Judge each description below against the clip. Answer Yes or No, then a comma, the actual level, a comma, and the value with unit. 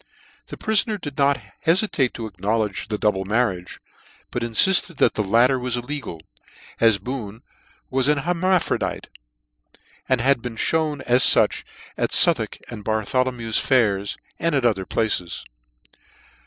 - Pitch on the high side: No, low, 120 Hz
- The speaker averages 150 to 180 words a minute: No, average, 140 wpm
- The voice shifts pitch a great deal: No, average, 4.9 semitones